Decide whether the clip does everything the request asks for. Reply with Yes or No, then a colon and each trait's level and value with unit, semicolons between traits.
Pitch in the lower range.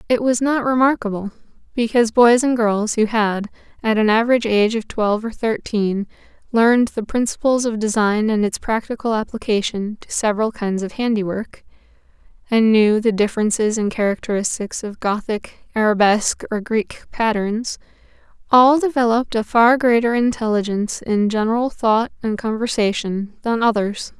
No: high, 220 Hz